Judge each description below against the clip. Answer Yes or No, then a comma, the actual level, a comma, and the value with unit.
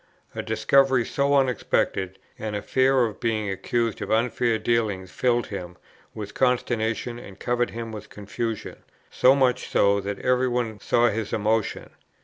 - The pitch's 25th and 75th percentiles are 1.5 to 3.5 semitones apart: Yes, average, 2.9 semitones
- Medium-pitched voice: No, low, 115 Hz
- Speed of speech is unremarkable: Yes, average, 150 wpm